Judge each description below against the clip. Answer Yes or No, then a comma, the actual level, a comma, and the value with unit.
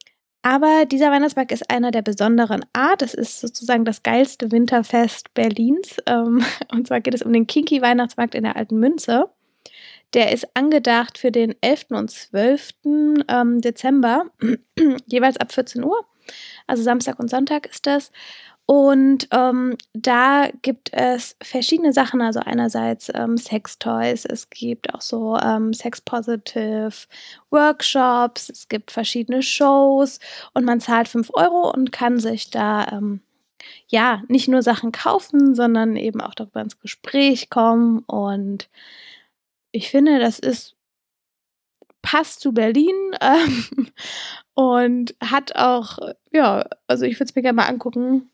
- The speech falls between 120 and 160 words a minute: Yes, average, 140 wpm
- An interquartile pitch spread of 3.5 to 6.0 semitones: No, average, 2.8 semitones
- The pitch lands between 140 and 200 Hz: No, high, 245 Hz